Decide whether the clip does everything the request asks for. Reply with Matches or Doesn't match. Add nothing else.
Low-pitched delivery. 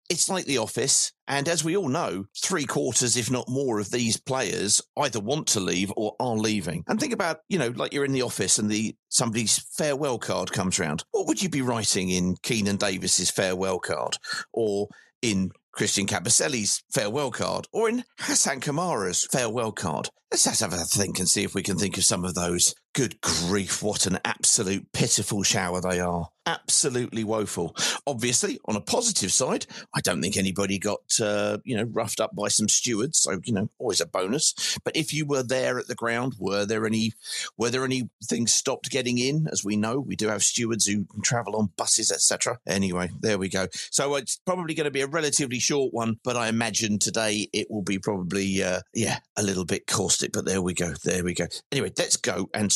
Matches